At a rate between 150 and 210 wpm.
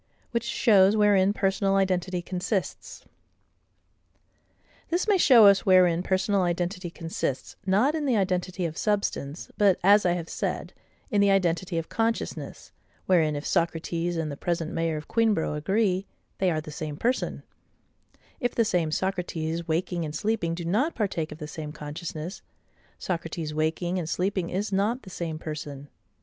Yes: average, 155 wpm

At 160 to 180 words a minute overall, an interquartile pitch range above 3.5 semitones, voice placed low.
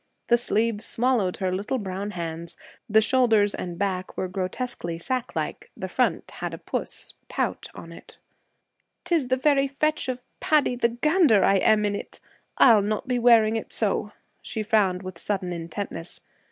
No: average, 165 wpm; average, 4.9 semitones; high, 215 Hz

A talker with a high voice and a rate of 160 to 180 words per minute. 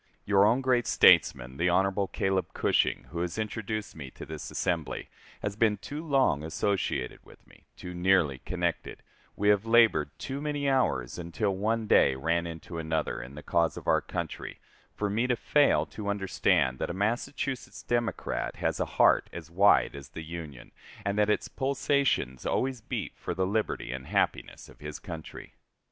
No: very low, 95 Hz; average, 175 wpm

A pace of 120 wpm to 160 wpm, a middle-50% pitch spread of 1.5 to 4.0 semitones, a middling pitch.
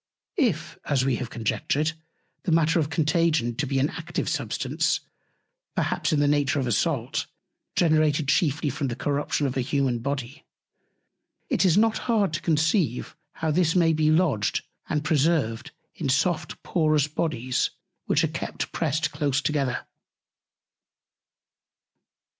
Yes: average, 140 wpm; average, 3.1 semitones; medium, 150 Hz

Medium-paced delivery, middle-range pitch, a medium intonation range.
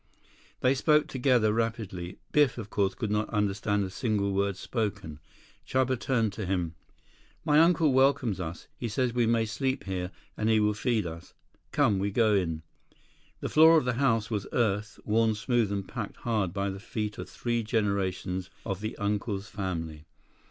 No: average, 175 wpm; low, 105 Hz; average, 3.5 semitones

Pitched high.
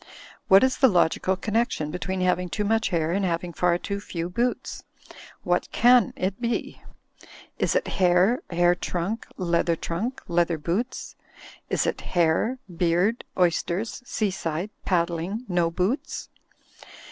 No: medium, 180 Hz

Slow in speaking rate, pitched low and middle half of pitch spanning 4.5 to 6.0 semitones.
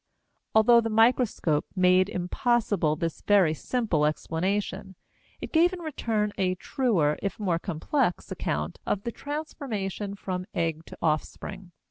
No: slow, 130 wpm; high, 195 Hz; average, 5.2 semitones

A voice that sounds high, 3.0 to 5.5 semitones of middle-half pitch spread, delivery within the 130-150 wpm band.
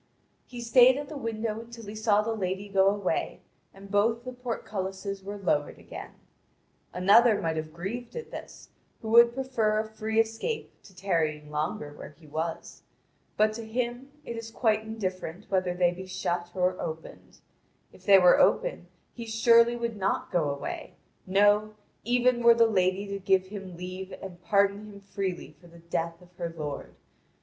No: high, 200 Hz; average, 4.0 semitones; average, 175 wpm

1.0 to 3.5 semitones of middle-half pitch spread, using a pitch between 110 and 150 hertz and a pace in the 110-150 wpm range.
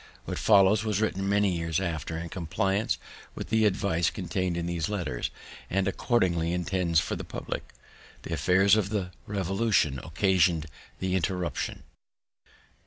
No: average, 2.8 semitones; very low, 95 Hz; average, 140 wpm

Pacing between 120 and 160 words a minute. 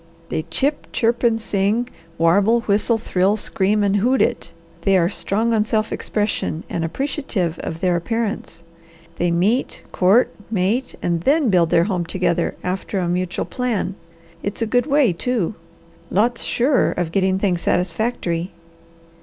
Yes: average, 150 wpm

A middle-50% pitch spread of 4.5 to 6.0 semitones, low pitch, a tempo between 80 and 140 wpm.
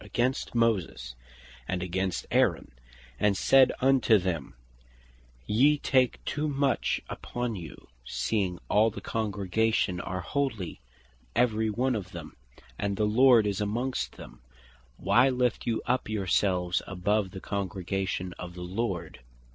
Yes: average, 4.8 semitones; low, 105 Hz; slow, 135 wpm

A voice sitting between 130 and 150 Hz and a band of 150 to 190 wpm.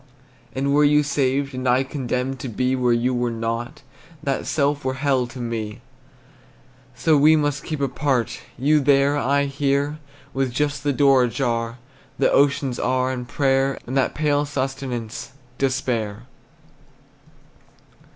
No: low, 135 Hz; average, 140 wpm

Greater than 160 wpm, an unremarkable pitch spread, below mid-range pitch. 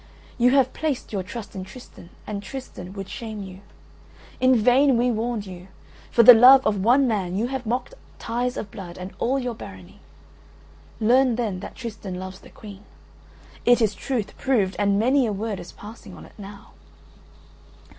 No: average, 175 wpm; average, 4.2 semitones; high, 220 Hz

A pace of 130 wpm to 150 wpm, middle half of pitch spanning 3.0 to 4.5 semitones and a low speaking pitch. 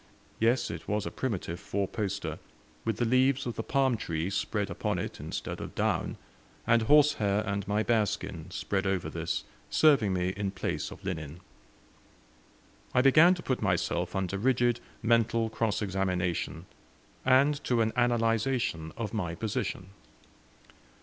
Yes: average, 145 wpm; average, 4.1 semitones; low, 110 Hz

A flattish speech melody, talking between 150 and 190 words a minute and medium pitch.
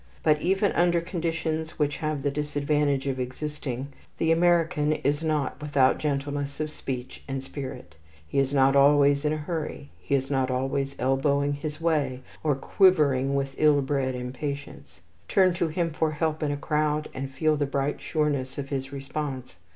Yes: narrow, 2.1 semitones; average, 170 wpm; medium, 145 Hz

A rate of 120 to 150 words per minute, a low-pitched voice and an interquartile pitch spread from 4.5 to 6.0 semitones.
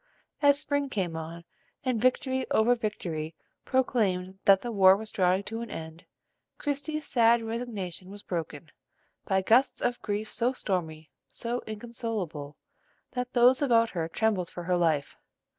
No: average, 145 wpm; high, 210 Hz; wide, 5.5 semitones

